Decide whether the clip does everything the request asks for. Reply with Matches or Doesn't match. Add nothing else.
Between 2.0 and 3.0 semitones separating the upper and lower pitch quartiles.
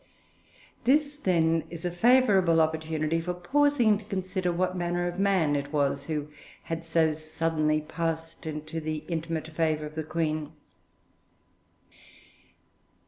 Matches